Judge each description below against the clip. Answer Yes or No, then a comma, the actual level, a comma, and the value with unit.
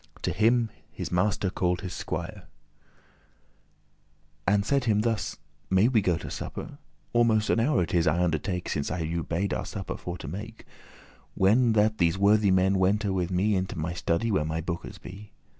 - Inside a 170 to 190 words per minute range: Yes, average, 180 wpm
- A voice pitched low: Yes, very low, 95 Hz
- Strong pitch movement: No, average, 3.5 semitones